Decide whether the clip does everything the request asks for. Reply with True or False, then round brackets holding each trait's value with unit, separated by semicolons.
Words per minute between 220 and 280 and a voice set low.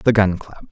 True (250 wpm; 100 Hz)